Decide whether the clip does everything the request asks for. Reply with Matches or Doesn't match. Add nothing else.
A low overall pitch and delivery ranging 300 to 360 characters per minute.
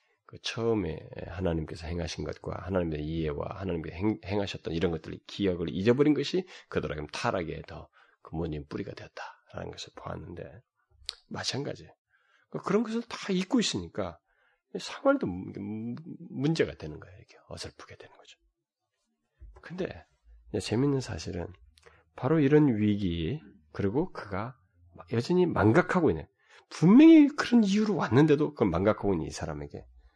Matches